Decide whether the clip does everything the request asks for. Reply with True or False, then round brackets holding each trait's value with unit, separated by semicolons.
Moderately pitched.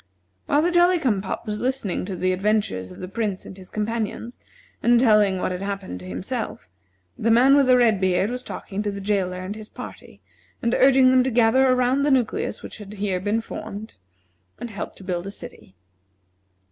False (210 Hz)